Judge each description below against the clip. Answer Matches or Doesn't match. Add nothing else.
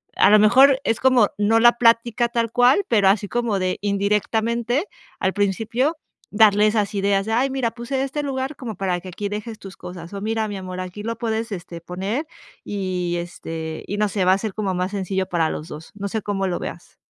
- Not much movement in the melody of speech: Doesn't match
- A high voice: Matches